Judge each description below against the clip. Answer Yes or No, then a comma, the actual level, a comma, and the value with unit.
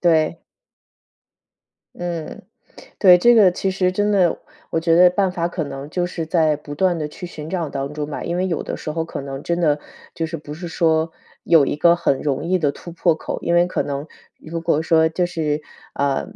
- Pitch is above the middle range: No, medium, 165 Hz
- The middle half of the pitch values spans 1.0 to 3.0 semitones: Yes, average, 2.7 semitones